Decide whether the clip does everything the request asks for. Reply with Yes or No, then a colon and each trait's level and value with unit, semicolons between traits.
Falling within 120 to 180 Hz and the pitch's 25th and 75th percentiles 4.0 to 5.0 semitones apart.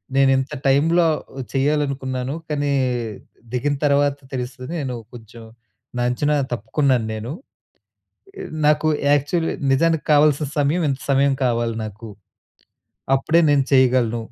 No: low, 135 Hz; average, 2.8 semitones